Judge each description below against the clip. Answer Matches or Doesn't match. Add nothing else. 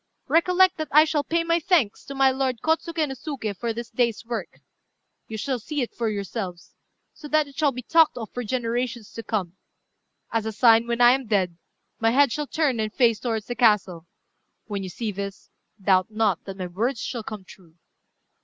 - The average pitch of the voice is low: Doesn't match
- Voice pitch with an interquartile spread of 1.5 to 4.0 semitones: Doesn't match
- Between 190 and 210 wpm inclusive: Matches